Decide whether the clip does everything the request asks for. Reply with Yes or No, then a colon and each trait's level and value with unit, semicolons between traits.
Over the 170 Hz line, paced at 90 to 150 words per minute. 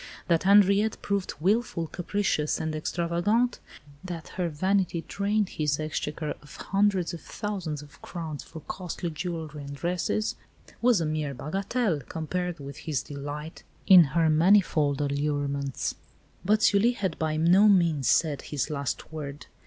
No: medium, 165 Hz; average, 140 wpm